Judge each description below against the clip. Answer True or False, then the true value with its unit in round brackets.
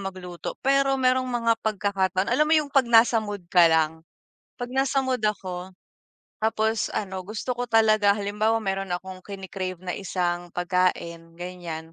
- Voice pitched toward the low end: False (200 Hz)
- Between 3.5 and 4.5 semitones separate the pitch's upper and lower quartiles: True (4.1 semitones)